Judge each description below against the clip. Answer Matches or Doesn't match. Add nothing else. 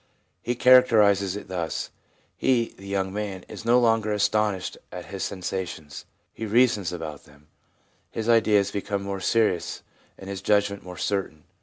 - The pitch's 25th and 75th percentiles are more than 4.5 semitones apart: Doesn't match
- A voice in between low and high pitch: Doesn't match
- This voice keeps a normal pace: Matches